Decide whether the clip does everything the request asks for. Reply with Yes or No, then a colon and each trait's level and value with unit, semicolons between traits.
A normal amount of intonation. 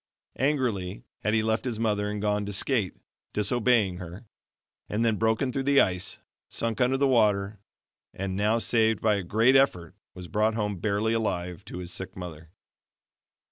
Yes: average, 3.4 semitones